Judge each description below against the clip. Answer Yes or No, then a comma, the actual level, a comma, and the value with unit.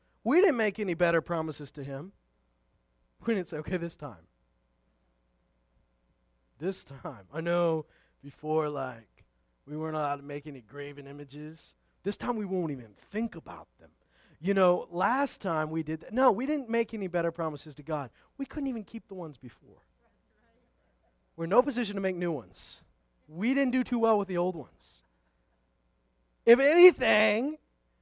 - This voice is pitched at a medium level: Yes, medium, 155 Hz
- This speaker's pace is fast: No, average, 165 wpm